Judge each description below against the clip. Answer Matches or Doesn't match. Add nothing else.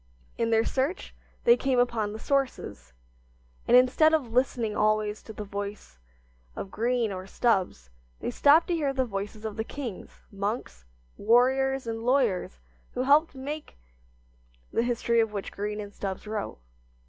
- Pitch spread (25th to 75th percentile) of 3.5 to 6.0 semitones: Matches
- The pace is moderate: Matches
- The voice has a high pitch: Matches